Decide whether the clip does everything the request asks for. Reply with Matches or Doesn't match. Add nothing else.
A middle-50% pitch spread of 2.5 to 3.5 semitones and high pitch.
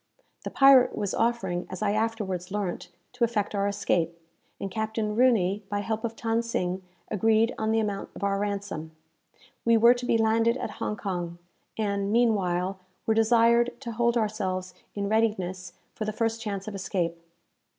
Matches